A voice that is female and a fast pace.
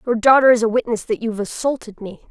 Yes: female; fast, 235 wpm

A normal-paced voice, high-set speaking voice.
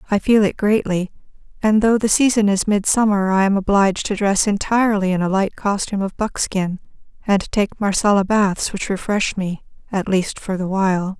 Yes: average, 180 wpm; high, 200 Hz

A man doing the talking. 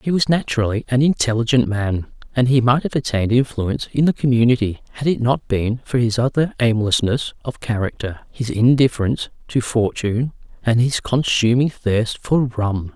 Yes: male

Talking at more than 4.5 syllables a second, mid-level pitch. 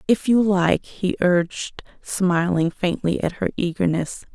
No: 4.0 syllables/s; medium, 180 Hz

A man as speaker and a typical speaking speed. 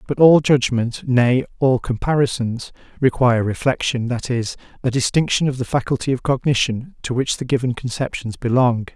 Yes: male; average, 155 wpm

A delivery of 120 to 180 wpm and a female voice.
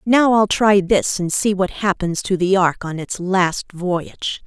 No: average, 200 wpm; female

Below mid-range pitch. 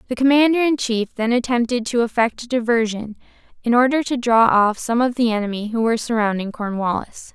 No: high, 235 Hz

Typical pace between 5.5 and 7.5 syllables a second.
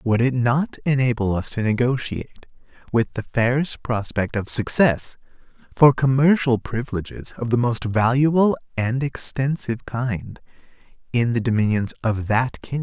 No: 4.7 syllables/s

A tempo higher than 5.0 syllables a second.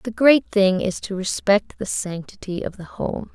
No: 4.4 syllables/s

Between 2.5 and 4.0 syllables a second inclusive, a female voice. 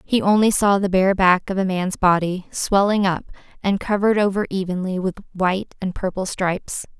No: 5.1 syllables/s; female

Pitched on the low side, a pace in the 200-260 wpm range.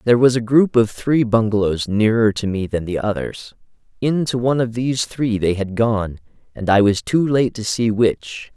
Yes: low, 115 Hz; fast, 205 wpm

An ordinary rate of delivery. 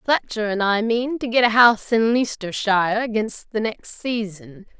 Yes: average, 175 wpm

